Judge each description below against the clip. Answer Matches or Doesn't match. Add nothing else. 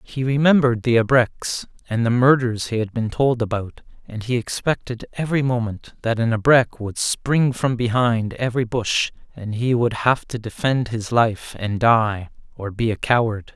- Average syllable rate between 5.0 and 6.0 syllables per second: Doesn't match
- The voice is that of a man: Matches